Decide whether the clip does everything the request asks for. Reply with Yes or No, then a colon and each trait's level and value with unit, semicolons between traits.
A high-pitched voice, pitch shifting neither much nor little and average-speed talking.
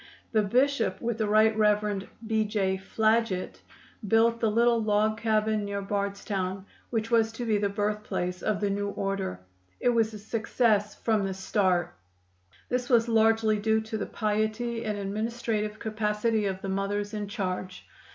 No: high, 215 Hz; narrow, 1.9 semitones; average, 160 wpm